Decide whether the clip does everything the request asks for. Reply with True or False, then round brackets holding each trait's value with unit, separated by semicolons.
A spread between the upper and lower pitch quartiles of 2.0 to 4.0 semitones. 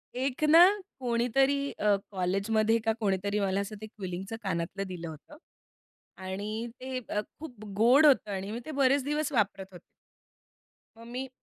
False (5.1 semitones)